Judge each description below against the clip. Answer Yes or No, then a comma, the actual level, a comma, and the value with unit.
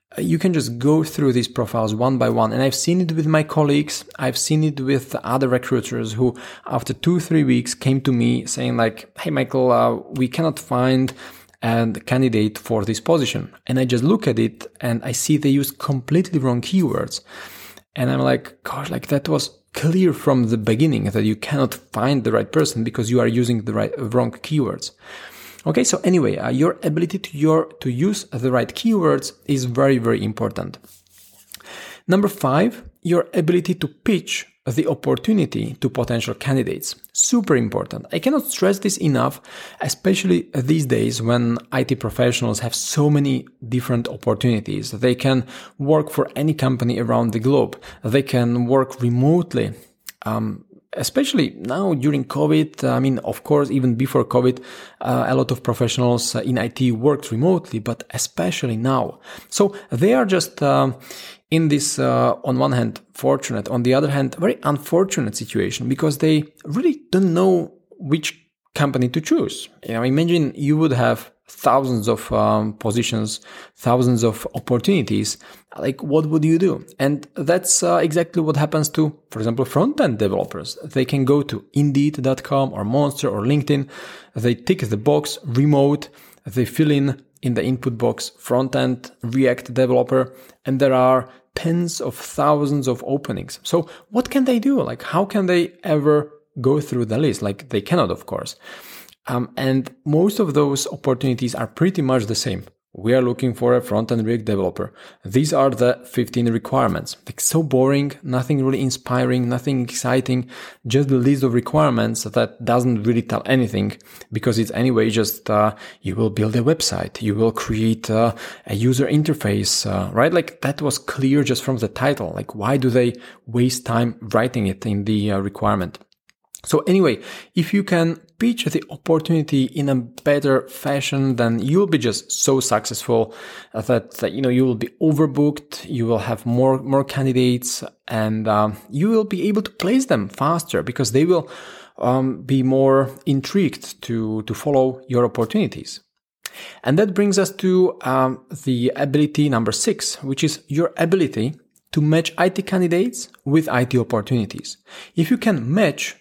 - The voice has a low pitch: Yes, low, 130 Hz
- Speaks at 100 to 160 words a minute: No, average, 170 wpm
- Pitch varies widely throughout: No, average, 4.5 semitones